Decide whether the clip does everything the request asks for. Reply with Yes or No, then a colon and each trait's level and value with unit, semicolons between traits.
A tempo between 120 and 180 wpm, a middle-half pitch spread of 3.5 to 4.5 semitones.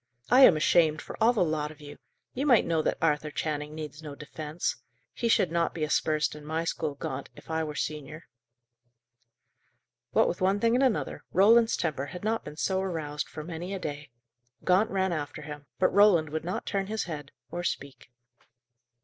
No: average, 190 wpm; average, 4.1 semitones